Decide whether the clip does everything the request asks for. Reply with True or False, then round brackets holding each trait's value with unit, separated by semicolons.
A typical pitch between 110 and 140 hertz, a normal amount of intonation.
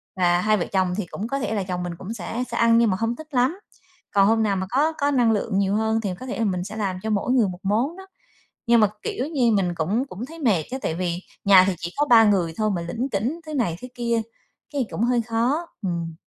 False (220 Hz; 4.5 semitones)